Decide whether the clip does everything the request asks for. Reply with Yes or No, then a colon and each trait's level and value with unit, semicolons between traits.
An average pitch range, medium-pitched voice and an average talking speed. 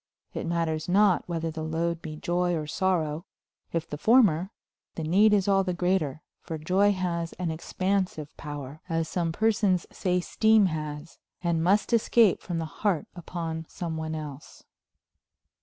Yes: average, 3.0 semitones; medium, 170 Hz; average, 155 wpm